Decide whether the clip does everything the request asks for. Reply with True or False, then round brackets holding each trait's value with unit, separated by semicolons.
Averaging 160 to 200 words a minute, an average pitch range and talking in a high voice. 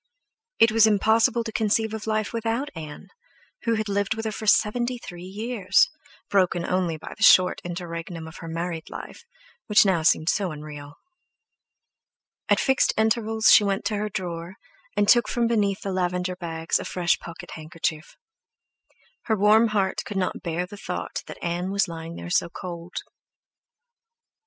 True (165 wpm; 4.3 semitones; 195 Hz)